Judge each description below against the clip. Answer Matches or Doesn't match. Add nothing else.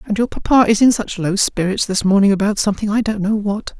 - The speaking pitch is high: Matches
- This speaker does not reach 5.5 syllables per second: Doesn't match